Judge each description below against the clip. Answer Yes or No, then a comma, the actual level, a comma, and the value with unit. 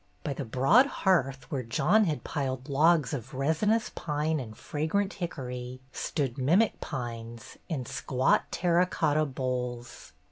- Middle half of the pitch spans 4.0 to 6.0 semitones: Yes, average, 4.5 semitones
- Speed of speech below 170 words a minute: Yes, slow, 135 wpm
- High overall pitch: No, medium, 140 Hz